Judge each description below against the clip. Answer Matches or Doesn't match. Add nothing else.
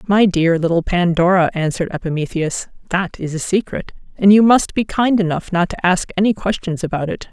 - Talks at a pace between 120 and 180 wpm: Doesn't match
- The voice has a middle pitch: Matches